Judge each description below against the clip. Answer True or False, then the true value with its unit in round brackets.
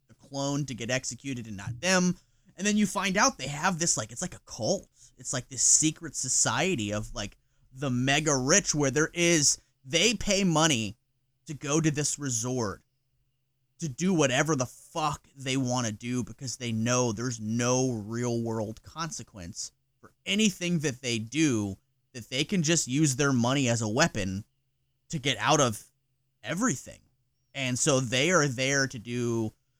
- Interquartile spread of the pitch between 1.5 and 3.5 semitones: False (3.9 semitones)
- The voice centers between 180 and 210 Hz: False (130 Hz)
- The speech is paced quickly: False (170 wpm)